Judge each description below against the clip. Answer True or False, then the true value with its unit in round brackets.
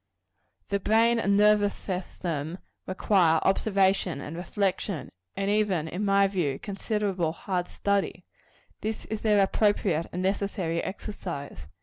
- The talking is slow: True (120 wpm)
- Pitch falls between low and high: False (195 Hz)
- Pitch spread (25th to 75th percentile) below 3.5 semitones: True (2.7 semitones)